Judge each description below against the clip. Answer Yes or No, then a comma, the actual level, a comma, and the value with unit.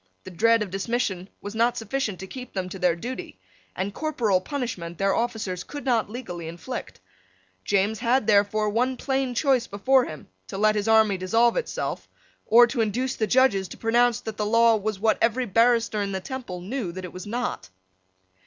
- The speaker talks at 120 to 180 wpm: No, average, 190 wpm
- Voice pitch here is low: No, high, 220 Hz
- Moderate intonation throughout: Yes, average, 3.9 semitones